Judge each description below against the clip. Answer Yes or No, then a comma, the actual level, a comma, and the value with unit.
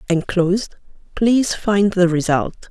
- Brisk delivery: No, slow, 110 wpm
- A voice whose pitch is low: No, high, 190 Hz